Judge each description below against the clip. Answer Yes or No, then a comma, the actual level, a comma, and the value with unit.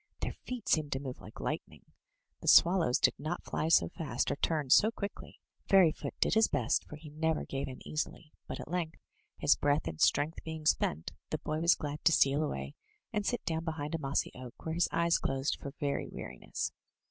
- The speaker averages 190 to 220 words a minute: Yes, fast, 205 wpm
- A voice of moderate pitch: Yes, medium, 155 Hz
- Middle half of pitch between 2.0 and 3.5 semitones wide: Yes, average, 2.9 semitones